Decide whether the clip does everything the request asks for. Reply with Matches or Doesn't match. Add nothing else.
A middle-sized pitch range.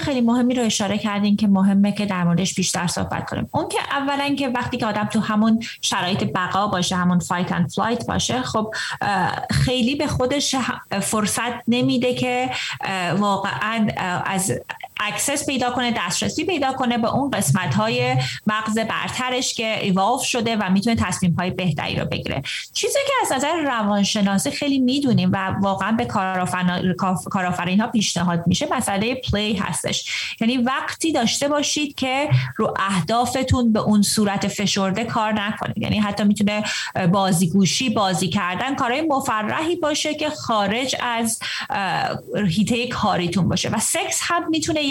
Matches